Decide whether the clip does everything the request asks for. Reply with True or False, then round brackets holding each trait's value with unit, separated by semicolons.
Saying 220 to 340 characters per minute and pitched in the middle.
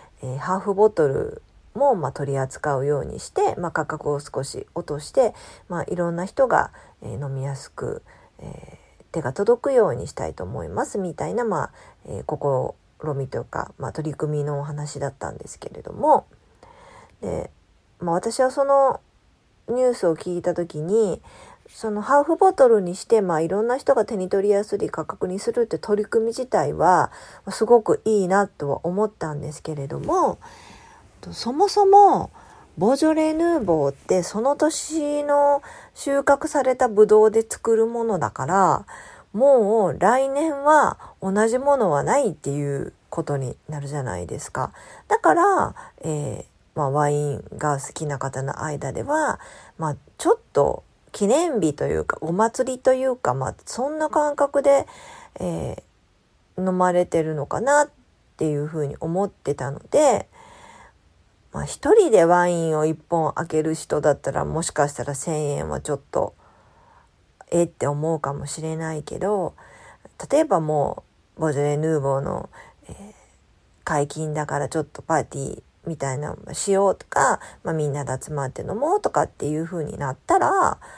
True (290 characters per minute; 180 Hz)